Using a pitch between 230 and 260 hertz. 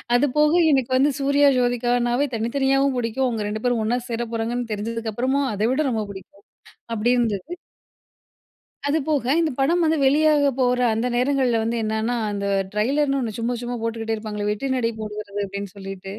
Yes: high, 240 Hz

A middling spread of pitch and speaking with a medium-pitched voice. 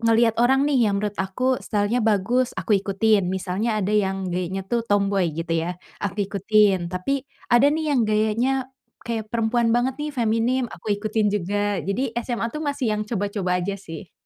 No: average, 3.6 semitones; high, 215 Hz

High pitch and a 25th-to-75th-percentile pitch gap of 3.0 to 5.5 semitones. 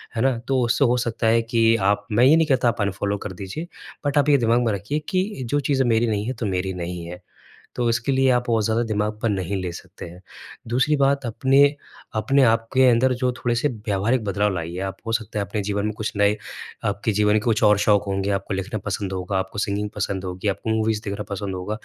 No: low, 110 Hz; average, 3.5 semitones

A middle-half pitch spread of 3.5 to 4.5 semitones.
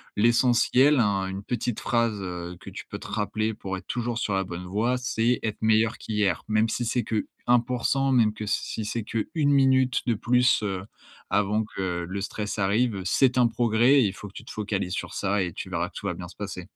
Yes: average, 3.8 semitones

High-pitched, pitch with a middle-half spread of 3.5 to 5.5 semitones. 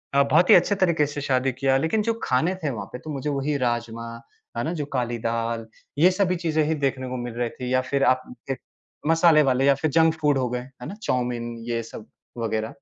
No: low, 135 Hz; average, 4.2 semitones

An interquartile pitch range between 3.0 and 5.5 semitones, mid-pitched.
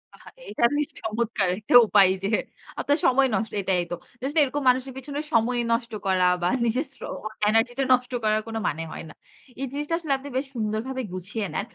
No: average, 4.0 semitones; high, 235 Hz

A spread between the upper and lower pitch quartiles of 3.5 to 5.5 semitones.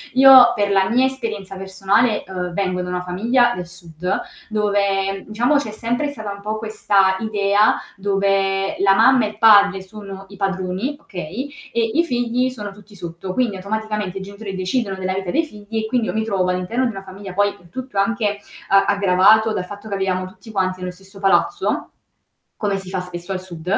No: narrow, 2.6 semitones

